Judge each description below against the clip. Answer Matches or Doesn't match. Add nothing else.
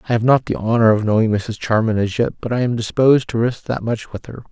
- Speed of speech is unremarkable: Doesn't match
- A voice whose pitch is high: Doesn't match